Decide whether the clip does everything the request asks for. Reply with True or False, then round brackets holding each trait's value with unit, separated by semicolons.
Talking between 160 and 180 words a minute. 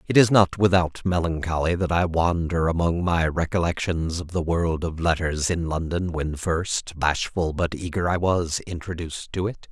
True (175 wpm)